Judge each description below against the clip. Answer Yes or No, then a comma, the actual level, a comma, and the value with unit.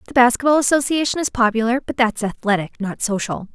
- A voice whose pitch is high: Yes, high, 235 Hz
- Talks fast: No, average, 185 wpm